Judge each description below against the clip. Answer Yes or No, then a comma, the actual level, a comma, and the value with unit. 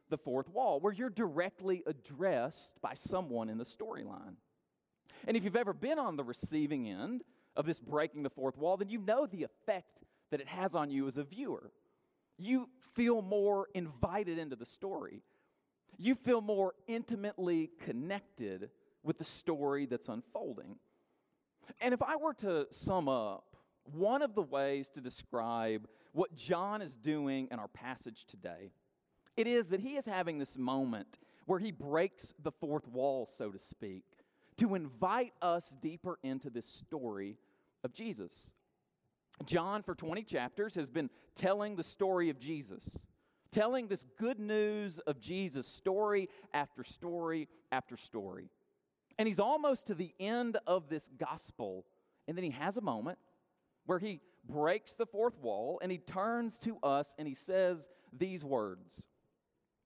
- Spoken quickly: No, average, 155 wpm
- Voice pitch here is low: No, medium, 180 Hz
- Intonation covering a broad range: Yes, wide, 7.6 semitones